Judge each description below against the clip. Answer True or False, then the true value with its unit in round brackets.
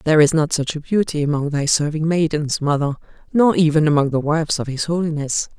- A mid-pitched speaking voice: True (155 Hz)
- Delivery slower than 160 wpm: False (205 wpm)